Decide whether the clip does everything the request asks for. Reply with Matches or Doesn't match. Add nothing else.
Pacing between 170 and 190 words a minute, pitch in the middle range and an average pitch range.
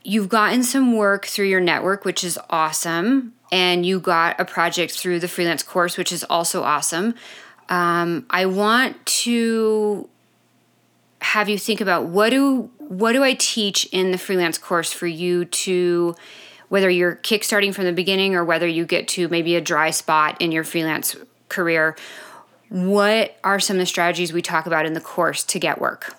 Matches